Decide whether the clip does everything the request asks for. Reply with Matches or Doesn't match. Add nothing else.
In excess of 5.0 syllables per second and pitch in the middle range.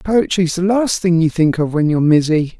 Matches